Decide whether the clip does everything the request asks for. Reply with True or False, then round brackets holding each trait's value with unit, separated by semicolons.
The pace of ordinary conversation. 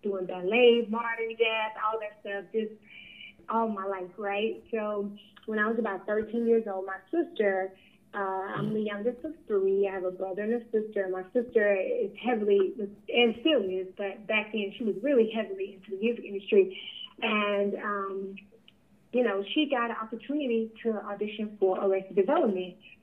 True (170 wpm)